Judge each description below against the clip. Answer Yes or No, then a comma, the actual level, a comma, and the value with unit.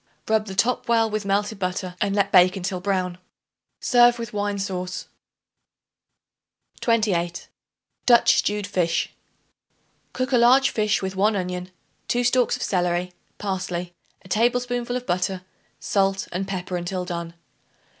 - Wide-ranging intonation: No, average, 3.6 semitones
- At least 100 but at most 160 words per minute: Yes, slow, 135 wpm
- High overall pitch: Yes, high, 195 Hz